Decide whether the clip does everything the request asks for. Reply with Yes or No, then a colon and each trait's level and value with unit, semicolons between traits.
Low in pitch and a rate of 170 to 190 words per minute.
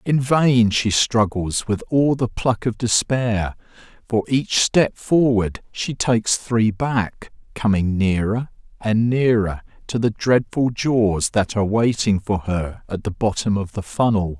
No: low, 110 Hz; average, 155 wpm